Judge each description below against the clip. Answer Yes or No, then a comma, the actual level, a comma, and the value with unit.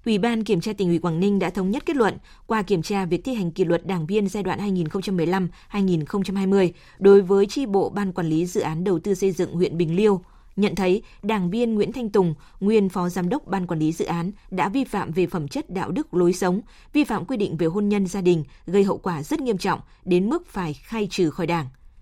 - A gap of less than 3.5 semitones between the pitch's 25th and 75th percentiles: Yes, average, 2.8 semitones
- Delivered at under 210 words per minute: No, average, 245 wpm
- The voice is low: No, high, 190 Hz